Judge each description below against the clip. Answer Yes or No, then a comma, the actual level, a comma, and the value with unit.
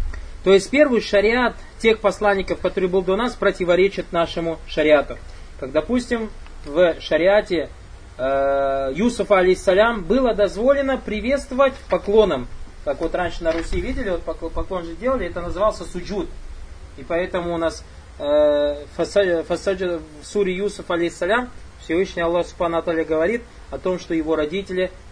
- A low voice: No, medium, 180 Hz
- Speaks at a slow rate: No, average, 135 wpm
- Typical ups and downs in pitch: Yes, average, 4.2 semitones